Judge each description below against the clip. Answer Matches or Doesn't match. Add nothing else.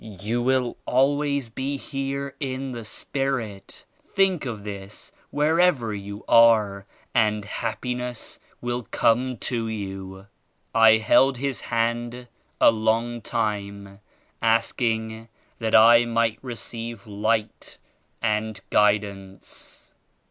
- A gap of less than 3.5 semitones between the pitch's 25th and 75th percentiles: Matches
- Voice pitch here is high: Doesn't match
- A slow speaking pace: Matches